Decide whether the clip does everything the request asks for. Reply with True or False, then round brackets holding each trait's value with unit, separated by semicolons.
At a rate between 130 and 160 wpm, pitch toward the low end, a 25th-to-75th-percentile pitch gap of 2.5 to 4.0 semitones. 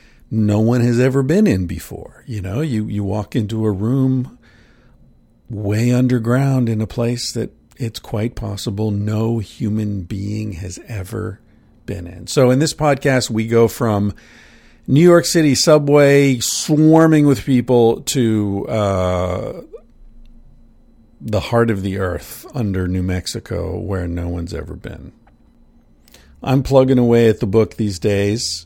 True (140 wpm; 115 Hz; 3.6 semitones)